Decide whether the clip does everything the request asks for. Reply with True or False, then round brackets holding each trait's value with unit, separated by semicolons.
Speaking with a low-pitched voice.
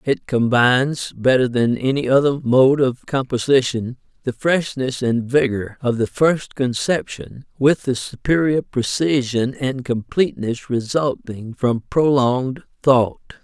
True (130 Hz)